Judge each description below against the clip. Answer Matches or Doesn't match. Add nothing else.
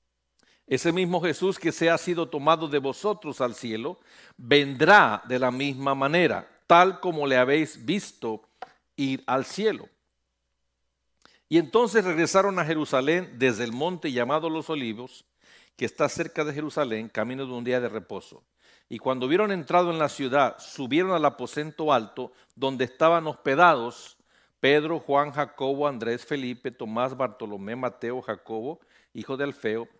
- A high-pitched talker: Doesn't match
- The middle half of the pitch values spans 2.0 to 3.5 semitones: Doesn't match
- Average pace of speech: Matches